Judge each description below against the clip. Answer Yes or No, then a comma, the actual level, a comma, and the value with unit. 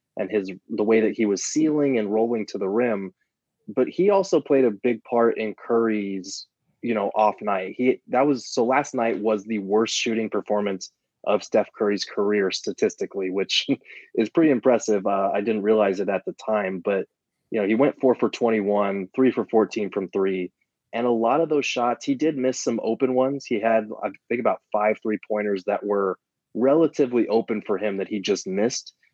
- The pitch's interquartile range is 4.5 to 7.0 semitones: No, average, 3.2 semitones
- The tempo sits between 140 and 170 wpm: No, average, 200 wpm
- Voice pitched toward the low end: Yes, low, 110 Hz